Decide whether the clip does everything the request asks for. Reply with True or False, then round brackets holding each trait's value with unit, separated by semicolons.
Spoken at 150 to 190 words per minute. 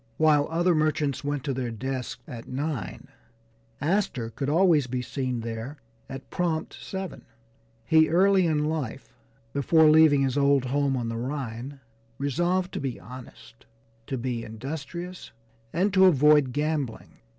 False (140 wpm)